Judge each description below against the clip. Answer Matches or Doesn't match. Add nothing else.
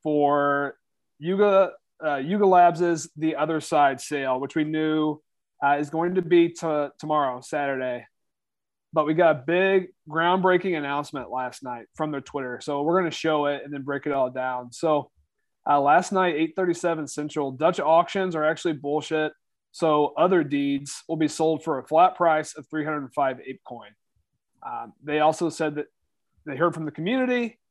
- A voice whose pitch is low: Doesn't match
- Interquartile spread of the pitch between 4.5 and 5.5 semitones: Doesn't match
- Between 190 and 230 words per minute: Doesn't match